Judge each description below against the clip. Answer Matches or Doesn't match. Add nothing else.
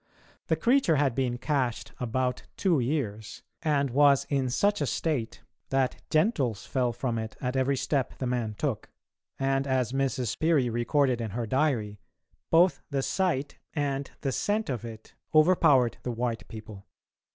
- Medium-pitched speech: Doesn't match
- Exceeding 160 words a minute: Doesn't match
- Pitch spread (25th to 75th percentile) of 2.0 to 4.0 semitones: Matches